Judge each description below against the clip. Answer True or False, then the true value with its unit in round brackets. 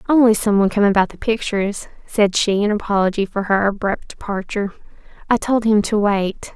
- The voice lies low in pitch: False (205 Hz)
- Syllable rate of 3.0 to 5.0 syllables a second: False (5.7 syllables/s)